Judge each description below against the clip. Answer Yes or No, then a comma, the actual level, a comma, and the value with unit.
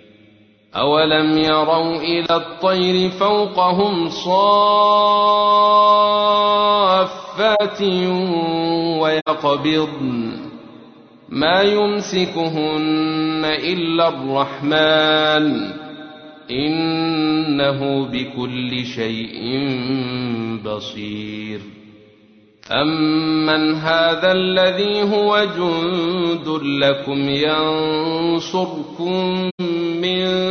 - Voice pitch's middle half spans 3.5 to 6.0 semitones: Yes, average, 4.7 semitones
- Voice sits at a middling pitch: Yes, medium, 155 Hz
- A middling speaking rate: No, slow, 45 wpm